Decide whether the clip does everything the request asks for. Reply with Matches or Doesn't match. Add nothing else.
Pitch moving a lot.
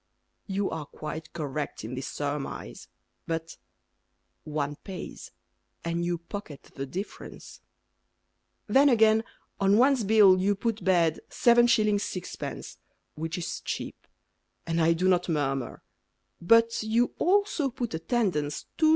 Matches